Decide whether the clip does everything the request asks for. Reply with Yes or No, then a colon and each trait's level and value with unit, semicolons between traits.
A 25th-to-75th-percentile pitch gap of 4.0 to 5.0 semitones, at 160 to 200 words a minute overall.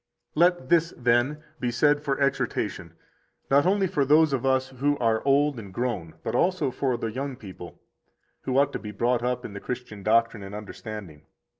Yes: average, 4.6 semitones; average, 190 wpm